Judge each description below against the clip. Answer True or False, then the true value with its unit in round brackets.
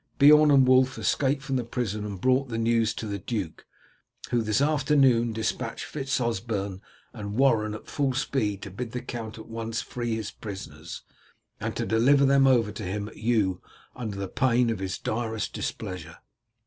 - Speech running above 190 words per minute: False (175 wpm)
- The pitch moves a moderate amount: True (3.8 semitones)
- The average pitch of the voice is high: False (115 Hz)